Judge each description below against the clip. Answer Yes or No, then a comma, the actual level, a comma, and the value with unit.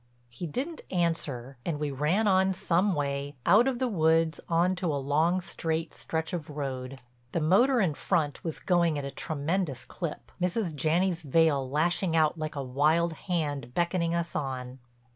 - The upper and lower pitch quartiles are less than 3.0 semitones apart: No, average, 3.7 semitones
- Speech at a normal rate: Yes, average, 170 wpm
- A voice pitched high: No, medium, 160 Hz